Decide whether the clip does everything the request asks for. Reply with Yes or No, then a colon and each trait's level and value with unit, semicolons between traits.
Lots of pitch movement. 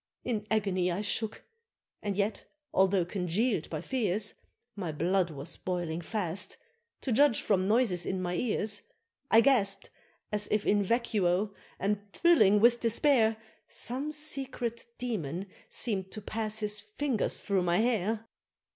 No: average, 3.7 semitones